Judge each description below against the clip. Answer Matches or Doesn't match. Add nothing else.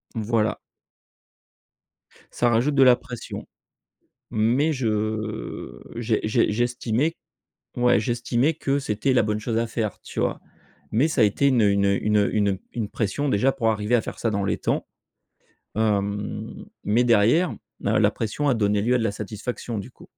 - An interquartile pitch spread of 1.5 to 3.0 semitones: Matches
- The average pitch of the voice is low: Matches